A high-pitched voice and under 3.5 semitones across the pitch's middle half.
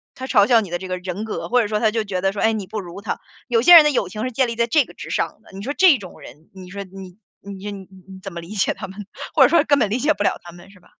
No: high, 205 Hz; average, 3.8 semitones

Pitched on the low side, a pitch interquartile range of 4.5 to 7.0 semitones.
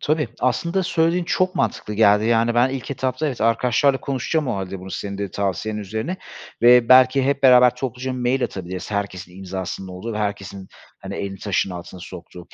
Yes: low, 115 Hz; average, 5.1 semitones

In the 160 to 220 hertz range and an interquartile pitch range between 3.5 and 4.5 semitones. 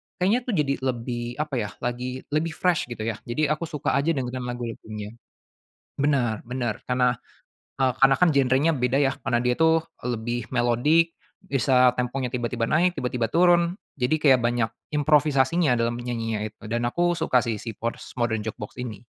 No: low, 125 Hz; average, 4.0 semitones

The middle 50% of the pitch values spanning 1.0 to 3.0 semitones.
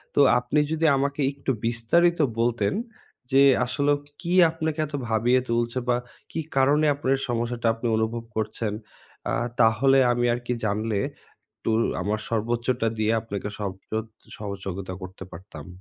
No: average, 3.8 semitones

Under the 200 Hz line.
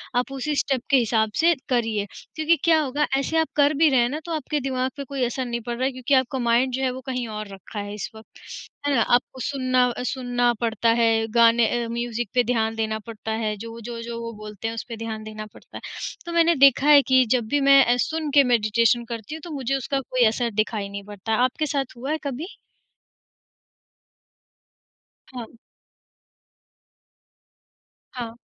No: high, 245 Hz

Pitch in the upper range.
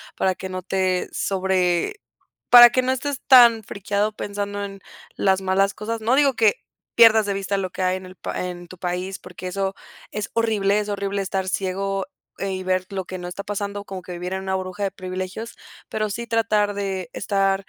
Yes: high, 195 Hz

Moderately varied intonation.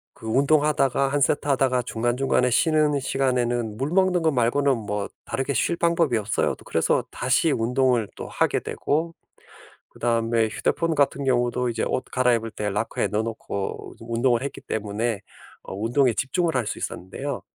Yes: average, 3.7 semitones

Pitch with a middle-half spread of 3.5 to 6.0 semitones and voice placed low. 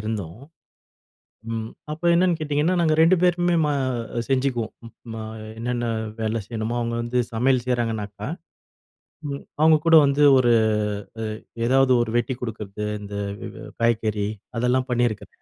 Yes: average, 3.9 semitones; low, 120 Hz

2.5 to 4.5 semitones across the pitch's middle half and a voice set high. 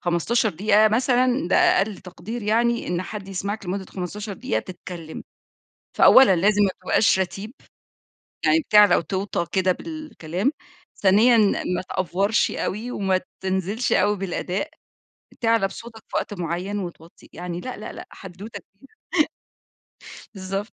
Yes: average, 3.2 semitones; high, 195 Hz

